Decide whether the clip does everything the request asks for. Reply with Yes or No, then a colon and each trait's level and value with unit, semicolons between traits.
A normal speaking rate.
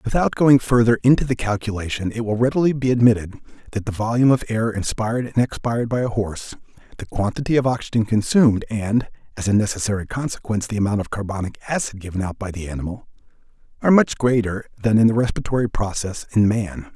Yes: average, 185 wpm